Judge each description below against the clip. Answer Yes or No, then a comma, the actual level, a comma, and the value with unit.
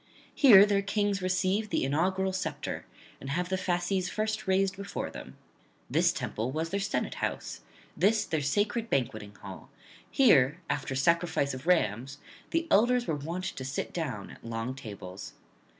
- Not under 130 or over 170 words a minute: Yes, average, 155 wpm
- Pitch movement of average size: No, wide, 6.7 semitones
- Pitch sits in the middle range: Yes, medium, 175 Hz